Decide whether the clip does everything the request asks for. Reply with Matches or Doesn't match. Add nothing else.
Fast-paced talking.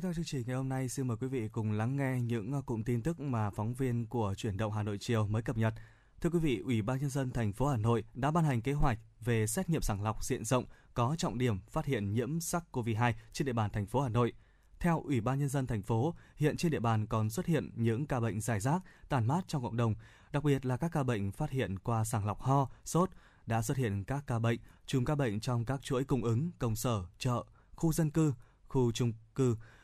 Matches